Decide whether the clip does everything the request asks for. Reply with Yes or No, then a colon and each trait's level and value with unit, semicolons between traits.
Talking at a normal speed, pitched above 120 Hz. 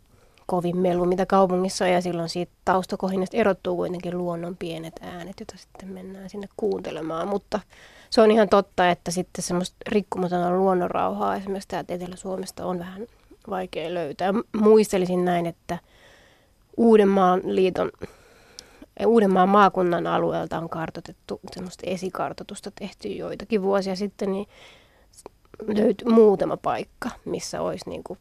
Yes: average, 130 wpm; high, 190 Hz